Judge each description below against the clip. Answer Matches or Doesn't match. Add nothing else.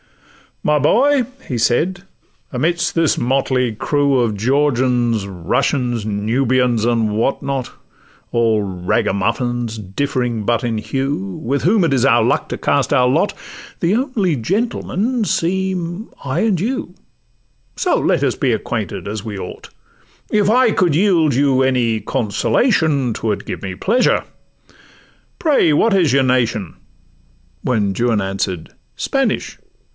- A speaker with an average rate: Doesn't match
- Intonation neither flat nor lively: Doesn't match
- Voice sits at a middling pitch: Doesn't match